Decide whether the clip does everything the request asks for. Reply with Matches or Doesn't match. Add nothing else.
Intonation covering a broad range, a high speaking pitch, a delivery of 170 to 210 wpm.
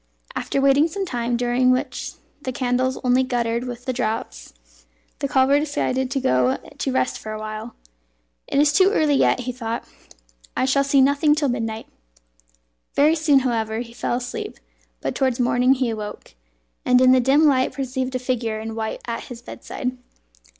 Doesn't match